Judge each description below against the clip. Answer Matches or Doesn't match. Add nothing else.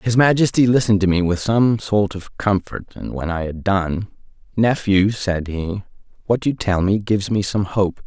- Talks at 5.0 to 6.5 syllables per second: Doesn't match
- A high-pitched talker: Doesn't match